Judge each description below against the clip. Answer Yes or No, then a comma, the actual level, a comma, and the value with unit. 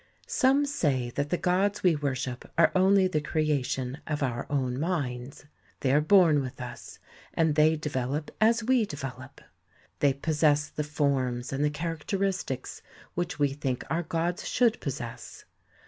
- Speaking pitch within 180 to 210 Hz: No, medium, 150 Hz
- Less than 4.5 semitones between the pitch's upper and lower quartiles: No, average, 4.8 semitones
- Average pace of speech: Yes, average, 150 wpm